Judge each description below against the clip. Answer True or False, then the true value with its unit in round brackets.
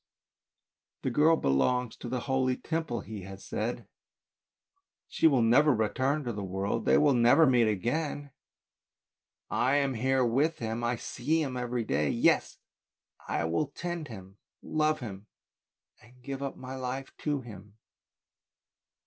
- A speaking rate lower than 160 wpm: True (150 wpm)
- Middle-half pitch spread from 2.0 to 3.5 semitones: False (4.2 semitones)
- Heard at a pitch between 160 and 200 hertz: False (125 Hz)